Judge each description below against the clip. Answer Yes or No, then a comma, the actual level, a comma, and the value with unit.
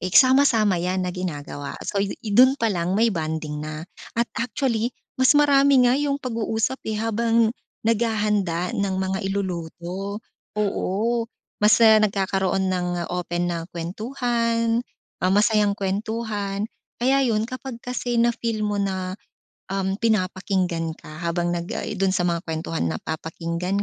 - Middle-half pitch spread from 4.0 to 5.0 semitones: Yes, average, 4.4 semitones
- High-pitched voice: Yes, high, 200 Hz